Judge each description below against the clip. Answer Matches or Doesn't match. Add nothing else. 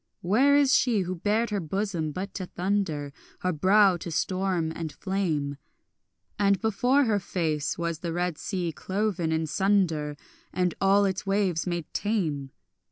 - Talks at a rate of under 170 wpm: Matches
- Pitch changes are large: Doesn't match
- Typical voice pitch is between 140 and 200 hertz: Matches